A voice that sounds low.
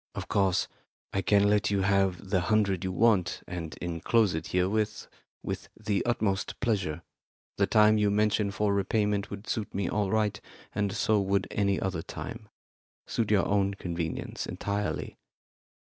Yes: low, 100 Hz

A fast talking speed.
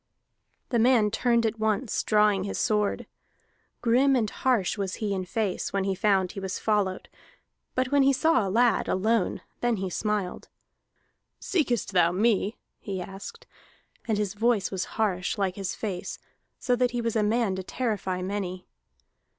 No: average, 165 wpm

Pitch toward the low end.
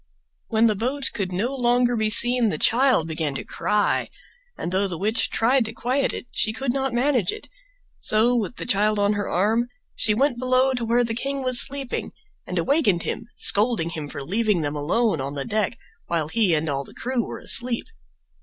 No: high, 225 Hz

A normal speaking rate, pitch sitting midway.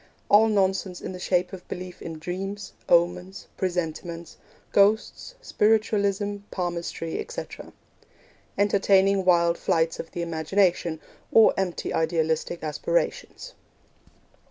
No: slow, 105 wpm; medium, 180 Hz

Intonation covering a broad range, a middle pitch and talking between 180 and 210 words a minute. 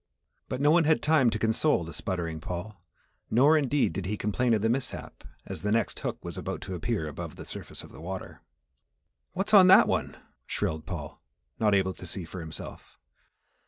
No: wide, 7.2 semitones; low, 105 Hz; average, 195 wpm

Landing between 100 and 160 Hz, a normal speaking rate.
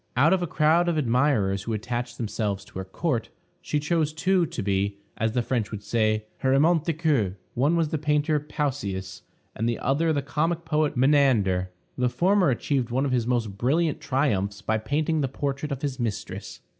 Yes: low, 135 Hz; average, 190 wpm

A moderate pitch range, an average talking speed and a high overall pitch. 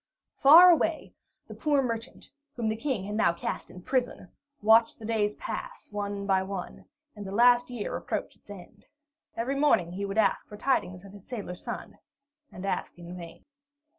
Yes: average, 4.3 semitones; average, 180 wpm; high, 210 Hz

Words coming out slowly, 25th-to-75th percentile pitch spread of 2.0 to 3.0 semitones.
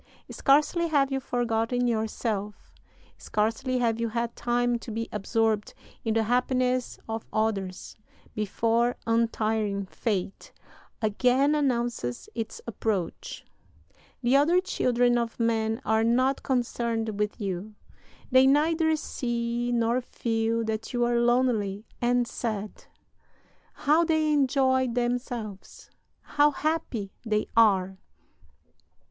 Yes: slow, 110 wpm; narrow, 2.5 semitones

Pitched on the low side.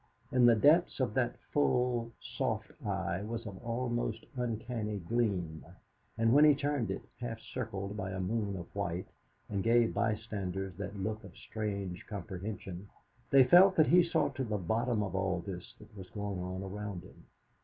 Yes: low, 105 Hz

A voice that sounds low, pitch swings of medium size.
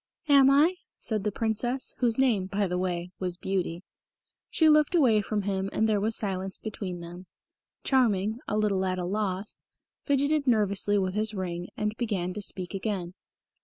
No: high, 205 Hz; average, 3.5 semitones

